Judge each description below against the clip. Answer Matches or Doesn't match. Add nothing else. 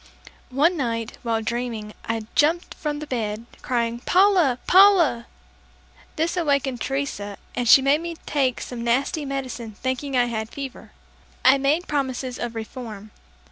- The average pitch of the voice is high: Matches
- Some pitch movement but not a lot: Matches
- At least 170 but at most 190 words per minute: Doesn't match